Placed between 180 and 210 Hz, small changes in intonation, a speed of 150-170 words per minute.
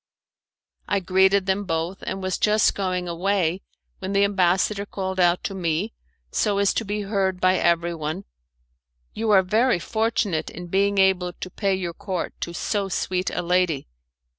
Yes: high, 190 Hz; narrow, 2.1 semitones; average, 165 wpm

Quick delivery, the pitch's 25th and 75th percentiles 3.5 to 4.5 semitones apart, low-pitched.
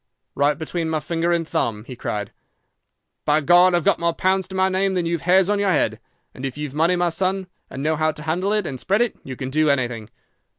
No: fast, 240 wpm; average, 4.2 semitones; medium, 165 Hz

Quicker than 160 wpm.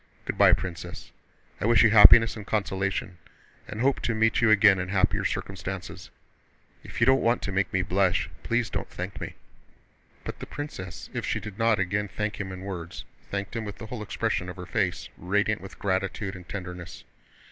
Yes: average, 190 wpm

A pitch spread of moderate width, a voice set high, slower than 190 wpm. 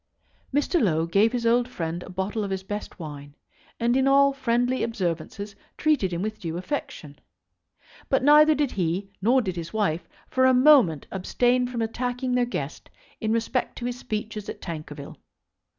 No: wide, 5.9 semitones; high, 220 Hz; average, 170 wpm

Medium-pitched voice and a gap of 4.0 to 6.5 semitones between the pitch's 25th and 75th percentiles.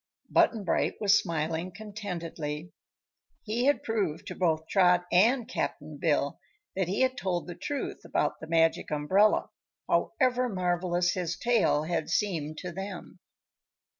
Yes: medium, 180 Hz; average, 4.4 semitones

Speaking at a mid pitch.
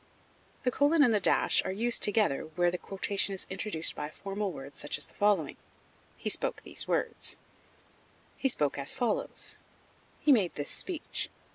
No: high, 200 Hz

